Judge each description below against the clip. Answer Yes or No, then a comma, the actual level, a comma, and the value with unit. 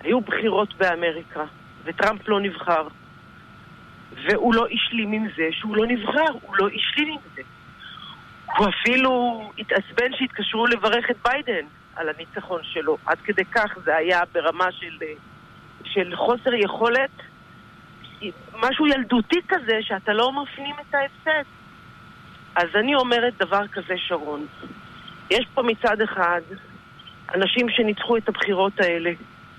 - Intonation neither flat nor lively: No, wide, 6.0 semitones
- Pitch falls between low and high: No, high, 205 Hz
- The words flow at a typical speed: Yes, average, 125 wpm